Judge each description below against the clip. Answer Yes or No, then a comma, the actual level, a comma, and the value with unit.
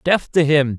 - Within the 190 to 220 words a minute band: No, fast, 230 wpm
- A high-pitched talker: No, medium, 150 Hz